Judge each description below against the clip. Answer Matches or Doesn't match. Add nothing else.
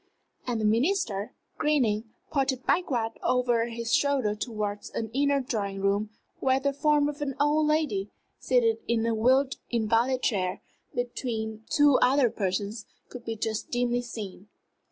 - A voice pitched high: Matches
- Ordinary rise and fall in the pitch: Matches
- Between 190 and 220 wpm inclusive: Doesn't match